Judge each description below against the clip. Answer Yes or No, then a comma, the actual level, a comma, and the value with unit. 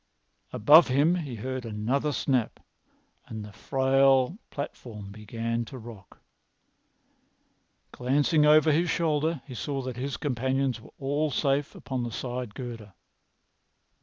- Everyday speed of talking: No, slow, 125 wpm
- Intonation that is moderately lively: Yes, average, 3.8 semitones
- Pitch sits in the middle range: No, low, 130 Hz